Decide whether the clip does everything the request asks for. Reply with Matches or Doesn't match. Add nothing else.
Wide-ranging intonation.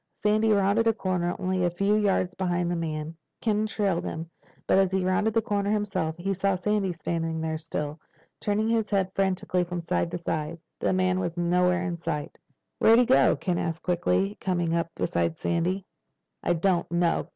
Doesn't match